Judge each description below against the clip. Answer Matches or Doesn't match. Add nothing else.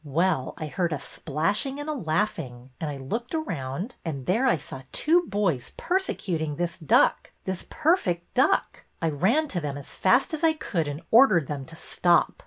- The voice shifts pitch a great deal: Matches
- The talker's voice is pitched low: Doesn't match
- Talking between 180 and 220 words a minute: Matches